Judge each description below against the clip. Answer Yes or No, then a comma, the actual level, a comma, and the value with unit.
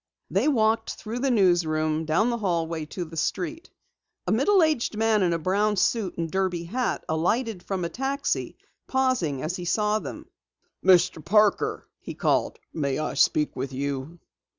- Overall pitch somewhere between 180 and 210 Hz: Yes, medium, 185 Hz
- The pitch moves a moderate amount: No, wide, 5.7 semitones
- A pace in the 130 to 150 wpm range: No, average, 165 wpm